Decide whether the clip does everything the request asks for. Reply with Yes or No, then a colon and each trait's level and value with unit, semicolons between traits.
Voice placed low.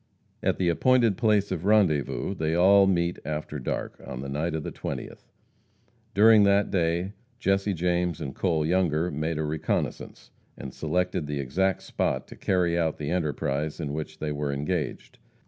Yes: very low, 85 Hz